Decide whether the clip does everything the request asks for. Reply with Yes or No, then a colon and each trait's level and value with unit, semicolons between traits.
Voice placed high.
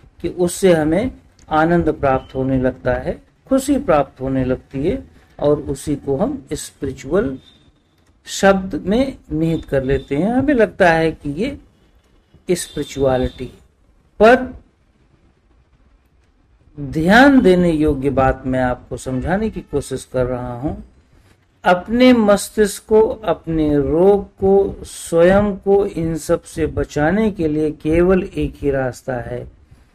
No: medium, 155 Hz